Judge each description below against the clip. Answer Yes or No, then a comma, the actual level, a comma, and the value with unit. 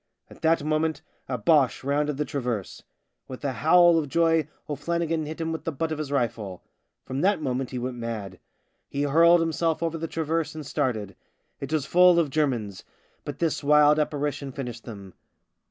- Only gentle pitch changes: No, average, 4.1 semitones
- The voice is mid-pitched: Yes, medium, 150 Hz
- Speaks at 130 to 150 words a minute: No, average, 200 wpm